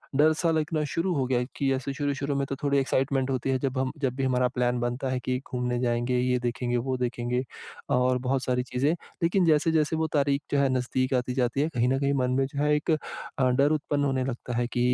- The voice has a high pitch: No, low, 130 Hz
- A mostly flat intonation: Yes, narrow, 2.2 semitones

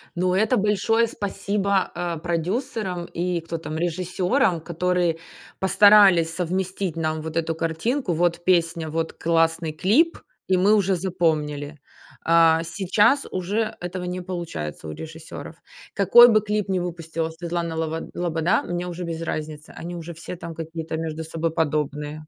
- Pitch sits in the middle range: Yes, medium, 170 Hz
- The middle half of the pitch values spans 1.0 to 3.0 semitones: Yes, average, 2.7 semitones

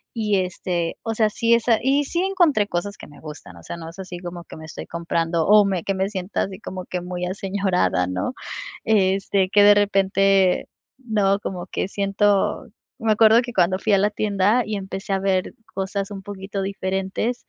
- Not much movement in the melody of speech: Yes, narrow, 2.3 semitones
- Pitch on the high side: Yes, high, 195 Hz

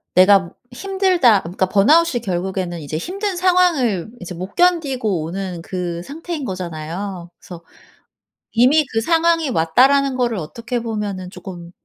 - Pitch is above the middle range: Yes, high, 210 Hz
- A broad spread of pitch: Yes, wide, 8.2 semitones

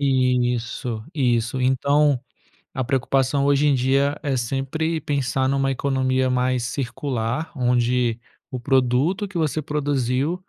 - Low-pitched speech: Yes, low, 130 Hz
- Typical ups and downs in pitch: No, narrow, 2.2 semitones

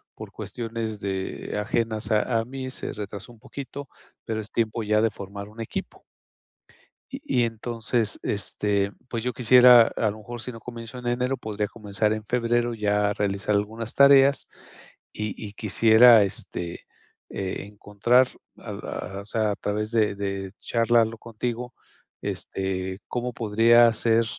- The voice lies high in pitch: No, low, 110 Hz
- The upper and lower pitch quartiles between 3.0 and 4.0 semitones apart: No, narrow, 2.5 semitones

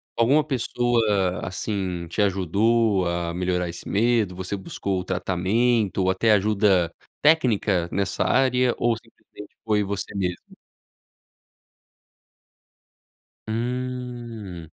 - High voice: No, low, 100 Hz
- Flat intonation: No, average, 4.3 semitones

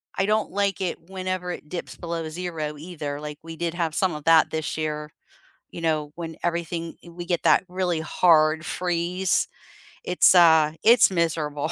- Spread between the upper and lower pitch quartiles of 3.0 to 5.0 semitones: No, narrow, 2.4 semitones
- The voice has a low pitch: No, medium, 170 Hz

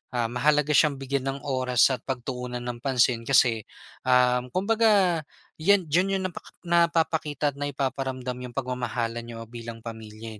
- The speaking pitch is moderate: No, low, 130 Hz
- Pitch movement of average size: Yes, average, 3.7 semitones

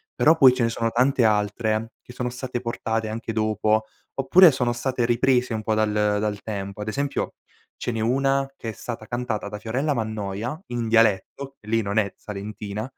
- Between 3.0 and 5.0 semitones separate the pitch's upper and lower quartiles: No, narrow, 2.6 semitones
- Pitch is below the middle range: Yes, low, 115 Hz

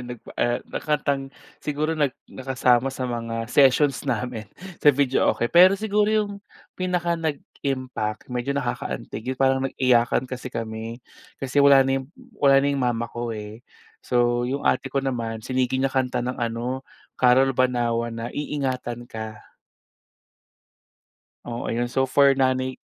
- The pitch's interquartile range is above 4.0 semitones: No, narrow, 2.4 semitones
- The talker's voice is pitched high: No, low, 130 Hz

